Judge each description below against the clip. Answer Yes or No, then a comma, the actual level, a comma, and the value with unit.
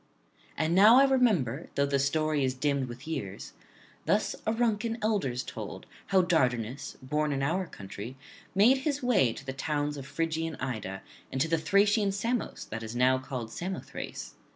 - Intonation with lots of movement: Yes, wide, 7.5 semitones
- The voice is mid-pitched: Yes, medium, 150 Hz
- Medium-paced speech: Yes, average, 170 wpm